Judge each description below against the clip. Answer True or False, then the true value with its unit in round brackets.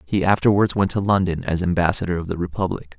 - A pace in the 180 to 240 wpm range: True (200 wpm)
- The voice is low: True (90 Hz)